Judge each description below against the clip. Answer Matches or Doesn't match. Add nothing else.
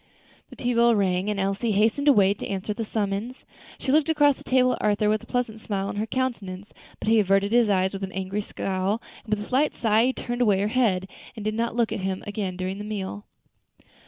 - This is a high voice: Matches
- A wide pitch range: Doesn't match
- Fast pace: Matches